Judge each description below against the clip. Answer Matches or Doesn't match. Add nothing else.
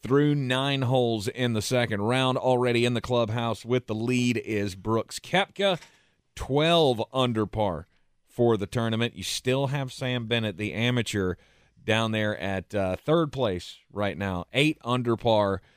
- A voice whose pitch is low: Matches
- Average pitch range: Matches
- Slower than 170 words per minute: Matches